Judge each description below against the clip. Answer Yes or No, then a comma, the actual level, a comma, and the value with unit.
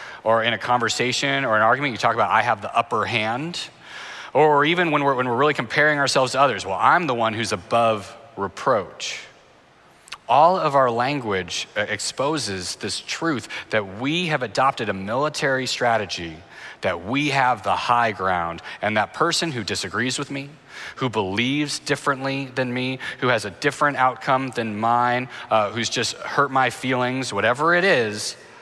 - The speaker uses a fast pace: No, average, 170 wpm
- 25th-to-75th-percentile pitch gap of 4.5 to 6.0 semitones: No, average, 3.8 semitones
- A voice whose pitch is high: No, low, 125 Hz